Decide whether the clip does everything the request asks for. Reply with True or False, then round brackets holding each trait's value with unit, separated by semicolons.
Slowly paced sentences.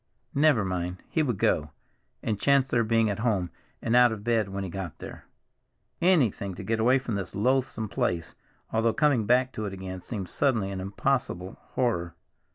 False (180 wpm)